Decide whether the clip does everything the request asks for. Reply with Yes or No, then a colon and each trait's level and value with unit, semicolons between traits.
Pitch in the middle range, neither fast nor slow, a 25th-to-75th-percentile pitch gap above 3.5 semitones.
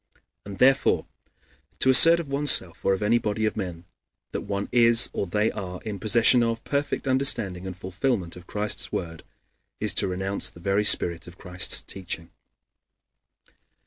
No: low, 100 Hz; average, 165 wpm; average, 4.5 semitones